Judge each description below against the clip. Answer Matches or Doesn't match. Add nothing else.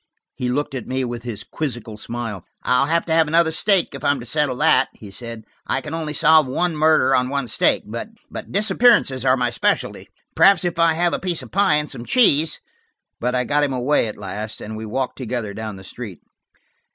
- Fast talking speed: Matches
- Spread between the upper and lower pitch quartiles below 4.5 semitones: Doesn't match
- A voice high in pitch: Doesn't match